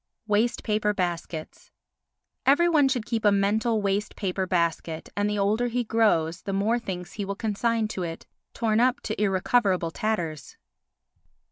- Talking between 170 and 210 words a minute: No, average, 150 wpm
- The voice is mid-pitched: No, high, 210 Hz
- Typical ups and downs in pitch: Yes, average, 3.6 semitones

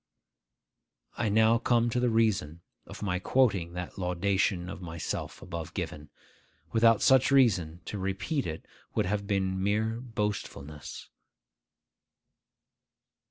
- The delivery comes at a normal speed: No, slow, 115 wpm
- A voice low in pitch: Yes, low, 100 Hz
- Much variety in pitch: No, average, 4.3 semitones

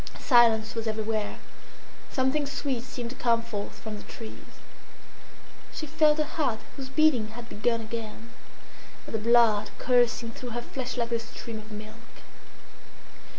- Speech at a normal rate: Yes, average, 150 wpm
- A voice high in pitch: Yes, high, 235 Hz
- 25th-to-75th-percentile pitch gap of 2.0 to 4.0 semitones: Yes, average, 2.9 semitones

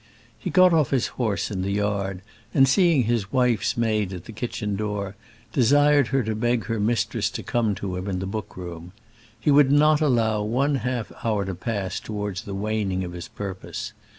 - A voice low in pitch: Yes, low, 110 Hz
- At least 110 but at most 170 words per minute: No, average, 195 wpm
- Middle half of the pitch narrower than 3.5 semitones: No, average, 4.1 semitones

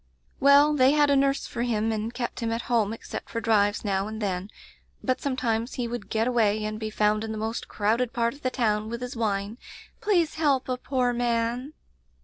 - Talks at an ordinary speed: No, fast, 215 wpm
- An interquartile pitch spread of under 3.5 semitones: Yes, average, 2.9 semitones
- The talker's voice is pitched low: No, high, 235 Hz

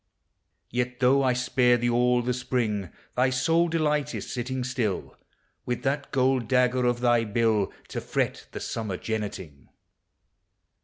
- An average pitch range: No, narrow, 2.2 semitones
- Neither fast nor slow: Yes, average, 145 wpm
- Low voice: Yes, low, 125 Hz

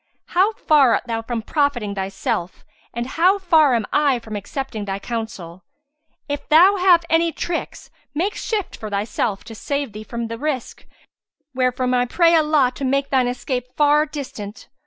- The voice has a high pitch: Yes, very high, 255 Hz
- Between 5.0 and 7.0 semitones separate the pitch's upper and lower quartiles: Yes, average, 5.3 semitones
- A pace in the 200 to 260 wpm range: No, average, 165 wpm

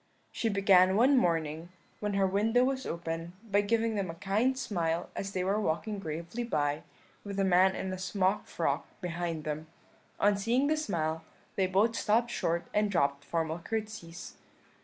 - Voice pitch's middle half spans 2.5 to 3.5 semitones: No, average, 4.3 semitones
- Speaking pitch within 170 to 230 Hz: Yes, high, 190 Hz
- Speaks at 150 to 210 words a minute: Yes, average, 170 wpm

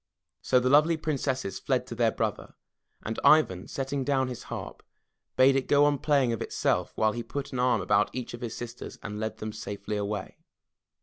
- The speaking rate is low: No, average, 195 wpm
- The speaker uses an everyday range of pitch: Yes, average, 4.2 semitones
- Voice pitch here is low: Yes, low, 125 Hz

